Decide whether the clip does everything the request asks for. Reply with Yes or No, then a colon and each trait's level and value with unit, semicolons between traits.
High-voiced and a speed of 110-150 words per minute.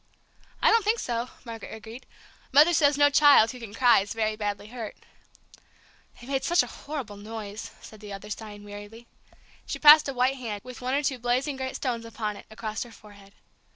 No: high, 230 Hz; average, 195 wpm